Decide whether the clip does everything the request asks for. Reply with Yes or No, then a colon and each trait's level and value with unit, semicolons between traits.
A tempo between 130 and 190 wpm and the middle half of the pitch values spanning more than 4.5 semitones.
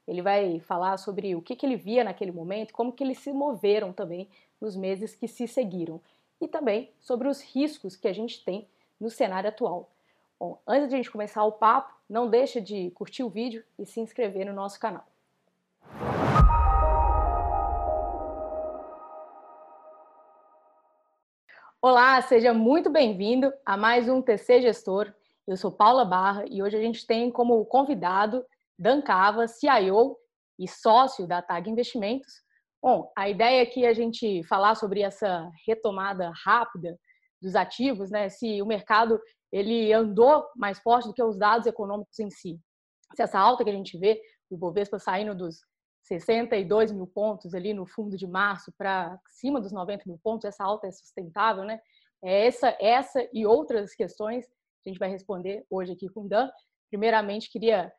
No: average, 160 wpm; average, 3.7 semitones